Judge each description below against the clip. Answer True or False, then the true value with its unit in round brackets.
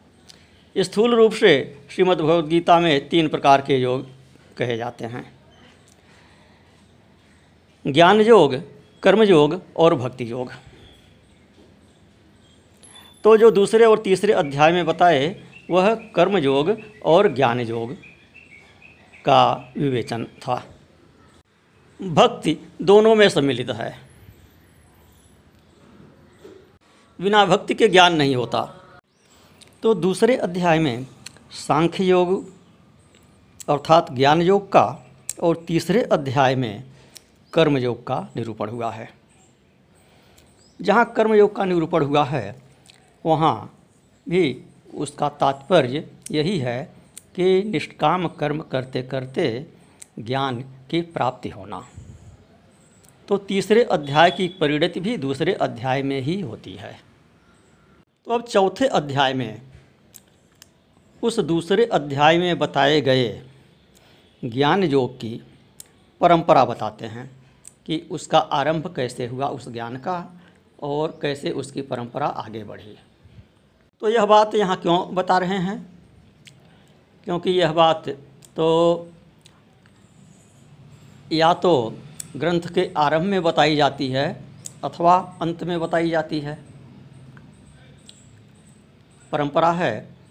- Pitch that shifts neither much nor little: False (5.7 semitones)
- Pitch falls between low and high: True (155 Hz)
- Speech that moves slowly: True (105 wpm)